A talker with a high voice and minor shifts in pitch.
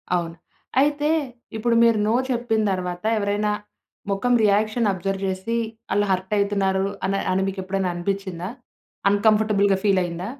Yes: high, 200 Hz; narrow, 2.3 semitones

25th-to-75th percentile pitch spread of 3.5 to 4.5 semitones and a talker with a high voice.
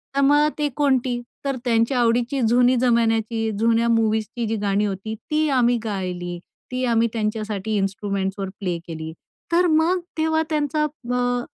Yes: average, 3.8 semitones; high, 235 Hz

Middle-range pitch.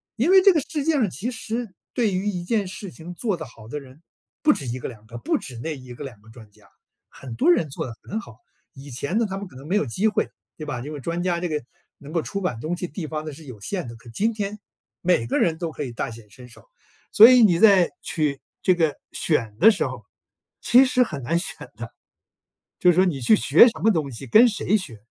Yes: medium, 165 Hz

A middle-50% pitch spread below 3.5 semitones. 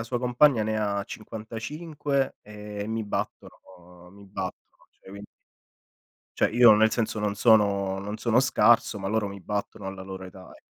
Yes: narrow, 2.4 semitones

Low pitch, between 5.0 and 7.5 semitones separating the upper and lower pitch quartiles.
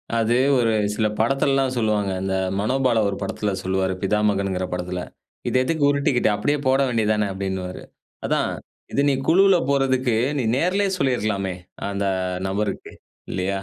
Yes: low, 110 Hz; wide, 5.4 semitones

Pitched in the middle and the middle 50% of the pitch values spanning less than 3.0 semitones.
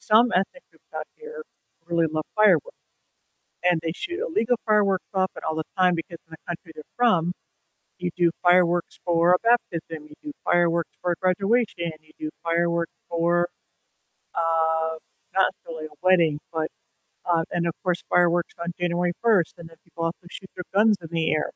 Yes: medium, 175 Hz; narrow, 2.4 semitones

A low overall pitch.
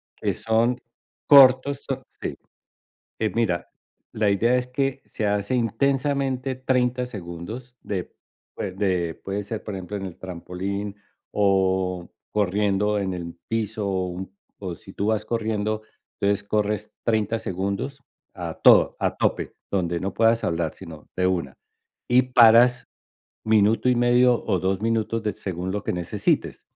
Yes: low, 105 Hz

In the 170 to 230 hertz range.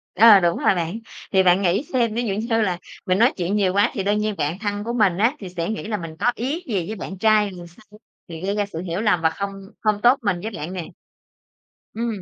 Yes: high, 205 Hz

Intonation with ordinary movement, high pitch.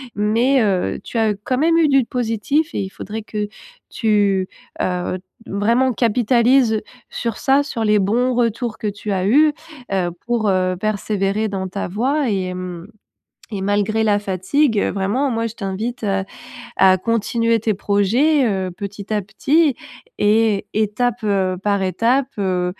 Yes: average, 3.5 semitones; high, 215 Hz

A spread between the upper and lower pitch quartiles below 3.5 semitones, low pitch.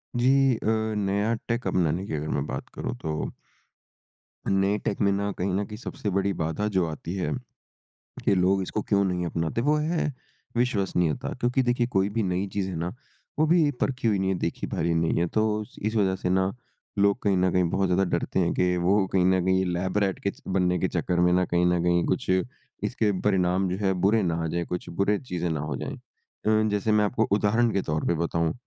Yes: average, 2.9 semitones; very low, 95 Hz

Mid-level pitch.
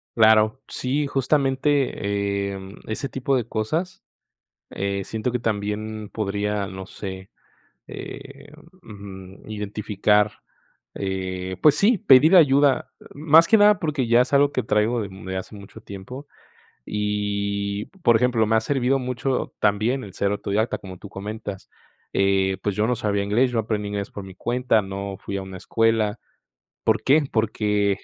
No: low, 105 Hz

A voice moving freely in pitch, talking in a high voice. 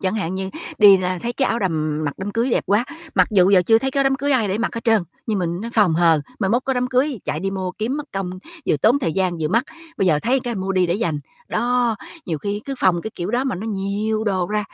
No: average, 4.5 semitones; high, 205 Hz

